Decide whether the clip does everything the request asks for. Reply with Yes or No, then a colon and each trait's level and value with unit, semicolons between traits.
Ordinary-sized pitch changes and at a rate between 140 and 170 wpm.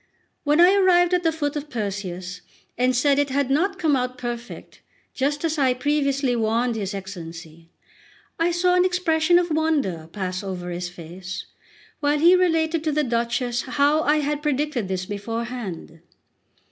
No: wide, 7.5 semitones; average, 160 wpm